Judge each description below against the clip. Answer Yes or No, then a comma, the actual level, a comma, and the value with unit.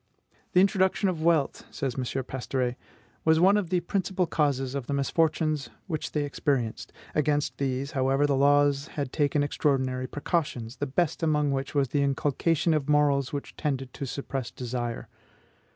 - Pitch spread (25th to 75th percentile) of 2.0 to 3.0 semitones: Yes, average, 2.7 semitones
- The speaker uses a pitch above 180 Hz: No, medium, 145 Hz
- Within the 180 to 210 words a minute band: No, average, 160 wpm